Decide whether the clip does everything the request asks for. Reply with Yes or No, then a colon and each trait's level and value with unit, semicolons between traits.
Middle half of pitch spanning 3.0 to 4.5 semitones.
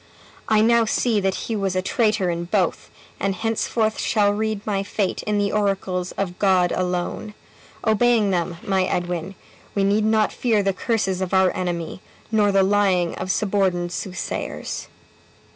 No: narrow, 2.6 semitones